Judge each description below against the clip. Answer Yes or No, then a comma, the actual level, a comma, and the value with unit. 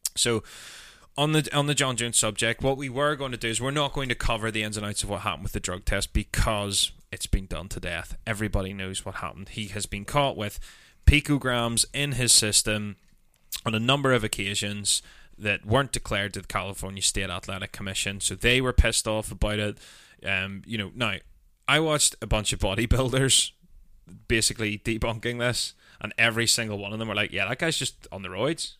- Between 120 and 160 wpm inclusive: No, fast, 205 wpm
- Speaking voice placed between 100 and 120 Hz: Yes, low, 110 Hz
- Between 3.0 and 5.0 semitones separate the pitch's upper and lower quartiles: Yes, average, 3.4 semitones